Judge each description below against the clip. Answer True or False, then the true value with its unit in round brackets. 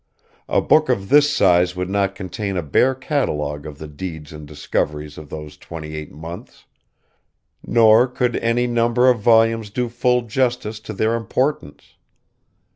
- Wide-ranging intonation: True (7.8 semitones)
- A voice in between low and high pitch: False (105 Hz)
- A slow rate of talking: False (155 wpm)